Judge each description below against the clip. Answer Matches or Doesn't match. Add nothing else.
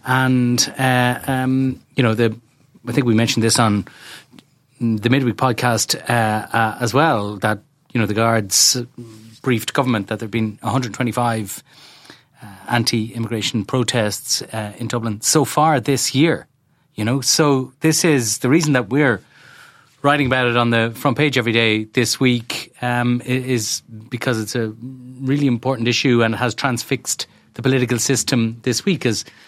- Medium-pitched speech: Doesn't match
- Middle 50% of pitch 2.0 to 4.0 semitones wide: Matches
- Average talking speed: Matches